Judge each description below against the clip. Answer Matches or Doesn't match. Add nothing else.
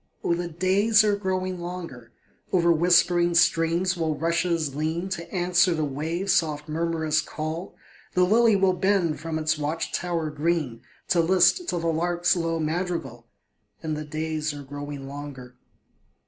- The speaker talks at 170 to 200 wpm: Doesn't match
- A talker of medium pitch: Matches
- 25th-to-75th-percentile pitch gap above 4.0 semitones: Doesn't match